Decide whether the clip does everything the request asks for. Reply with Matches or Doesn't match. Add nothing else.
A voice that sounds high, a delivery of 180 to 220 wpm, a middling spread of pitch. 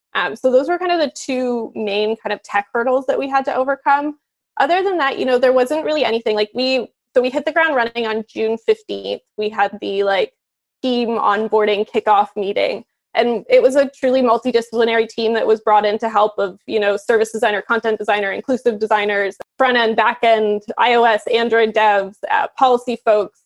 Matches